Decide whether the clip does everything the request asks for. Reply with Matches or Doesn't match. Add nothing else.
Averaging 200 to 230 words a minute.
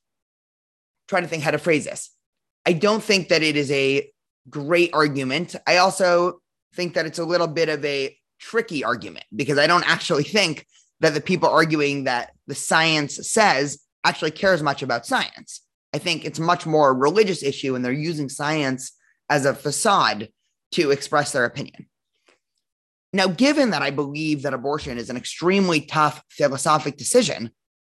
Doesn't match